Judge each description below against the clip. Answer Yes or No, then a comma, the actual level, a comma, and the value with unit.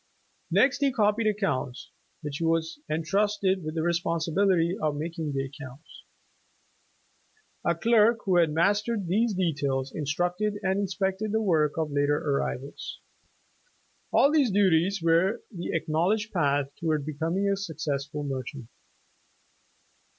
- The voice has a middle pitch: Yes, medium, 170 Hz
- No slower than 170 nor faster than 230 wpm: No, slow, 135 wpm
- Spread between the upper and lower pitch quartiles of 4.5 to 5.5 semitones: Yes, average, 5.1 semitones